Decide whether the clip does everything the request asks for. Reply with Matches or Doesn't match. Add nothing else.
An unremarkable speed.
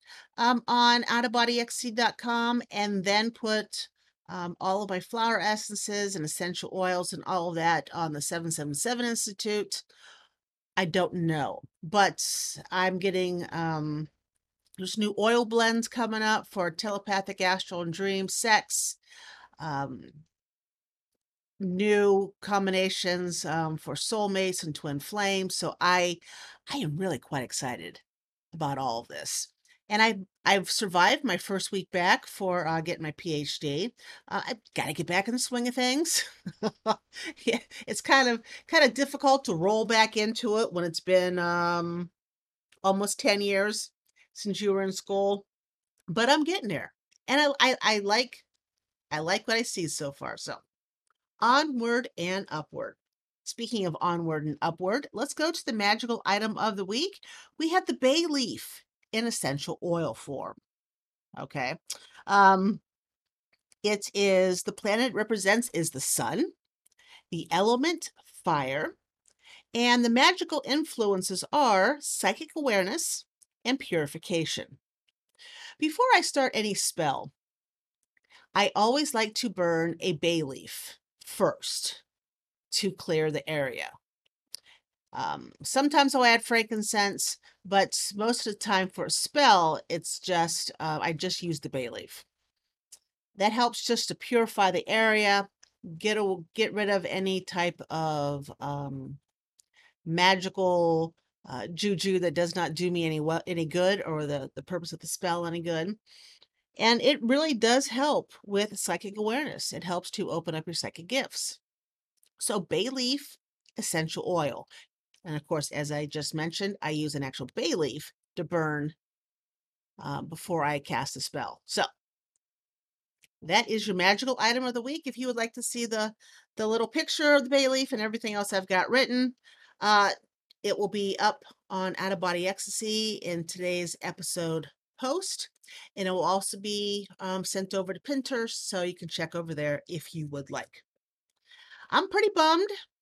Matches